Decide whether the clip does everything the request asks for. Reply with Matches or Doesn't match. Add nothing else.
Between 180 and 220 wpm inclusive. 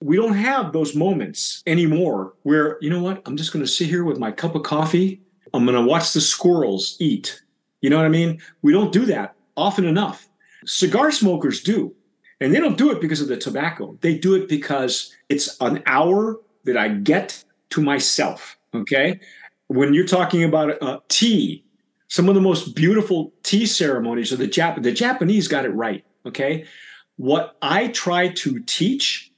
Matches